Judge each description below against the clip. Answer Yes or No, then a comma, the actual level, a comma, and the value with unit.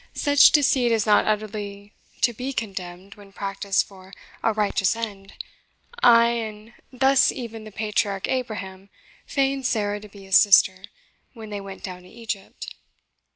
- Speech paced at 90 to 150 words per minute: Yes, average, 145 wpm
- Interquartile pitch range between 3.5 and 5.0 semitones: No, average, 2.9 semitones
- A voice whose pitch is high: Yes, high, 210 Hz